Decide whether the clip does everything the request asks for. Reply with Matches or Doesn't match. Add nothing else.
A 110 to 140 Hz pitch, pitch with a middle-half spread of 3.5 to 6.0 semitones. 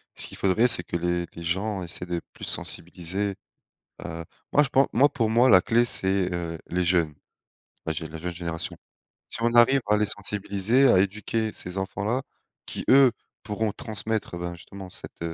Doesn't match